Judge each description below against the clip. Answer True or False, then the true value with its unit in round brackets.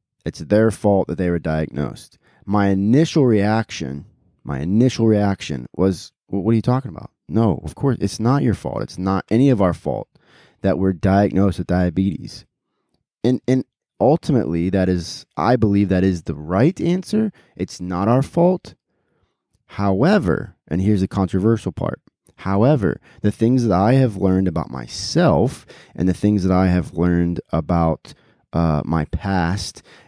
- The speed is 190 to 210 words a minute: False (160 wpm)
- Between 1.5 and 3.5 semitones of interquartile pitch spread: False (4.3 semitones)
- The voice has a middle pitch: False (95 Hz)